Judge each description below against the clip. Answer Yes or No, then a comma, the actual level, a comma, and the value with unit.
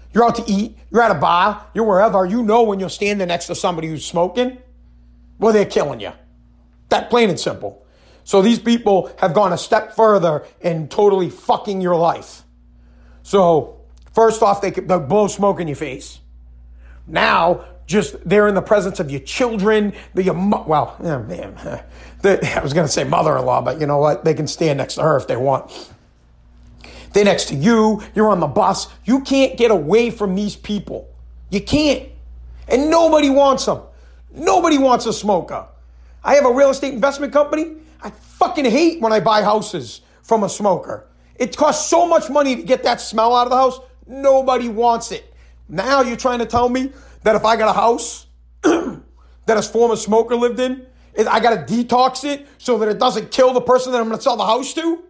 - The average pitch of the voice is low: No, high, 215 Hz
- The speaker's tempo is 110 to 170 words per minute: No, average, 195 wpm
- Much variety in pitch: Yes, wide, 7.0 semitones